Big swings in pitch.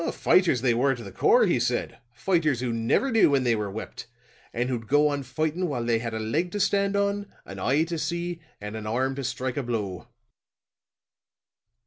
Yes: wide, 6.8 semitones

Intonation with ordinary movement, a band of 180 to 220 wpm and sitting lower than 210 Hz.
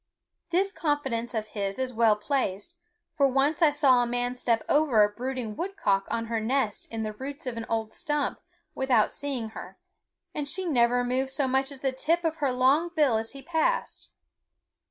No: average, 4.2 semitones; average, 190 wpm; very high, 260 Hz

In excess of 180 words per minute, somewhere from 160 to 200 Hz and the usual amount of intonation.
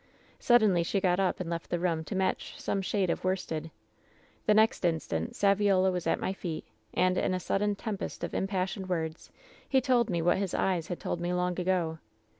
No: average, 200 wpm; medium, 185 Hz; narrow, 2.3 semitones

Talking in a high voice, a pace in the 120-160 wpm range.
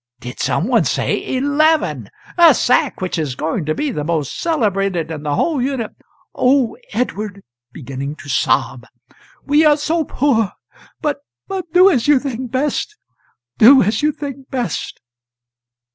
Yes: very high, 250 Hz; average, 155 wpm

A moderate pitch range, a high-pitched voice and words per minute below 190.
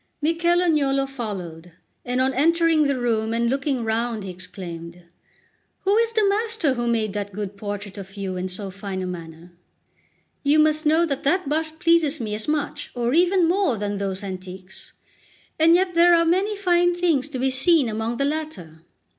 No: wide, 8.6 semitones; very high, 260 Hz; average, 180 wpm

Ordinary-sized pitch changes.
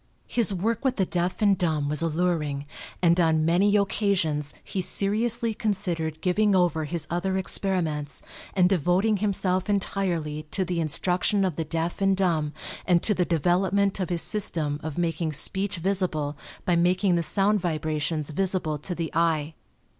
Yes: average, 3.5 semitones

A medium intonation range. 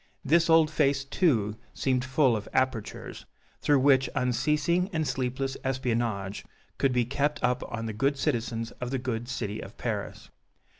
Yes: average, 3.2 semitones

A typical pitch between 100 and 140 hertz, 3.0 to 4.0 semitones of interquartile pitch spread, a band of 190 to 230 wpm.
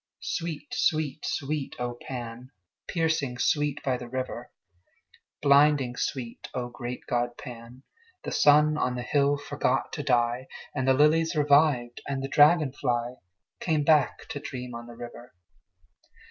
No: low, 135 Hz; average, 3.3 semitones; average, 145 wpm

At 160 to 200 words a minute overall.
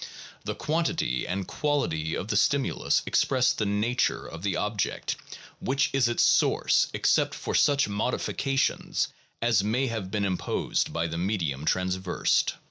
No: average, 140 wpm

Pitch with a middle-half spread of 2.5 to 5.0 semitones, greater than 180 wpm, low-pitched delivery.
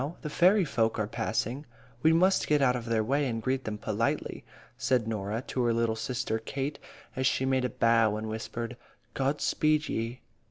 Yes: average, 3.5 semitones; average, 195 wpm; low, 125 Hz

